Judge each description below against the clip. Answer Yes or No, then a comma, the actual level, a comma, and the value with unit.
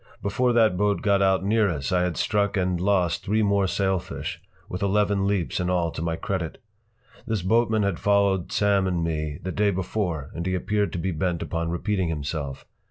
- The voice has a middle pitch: No, very low, 95 Hz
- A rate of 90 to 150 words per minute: No, average, 195 wpm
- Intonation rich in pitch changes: No, average, 3.0 semitones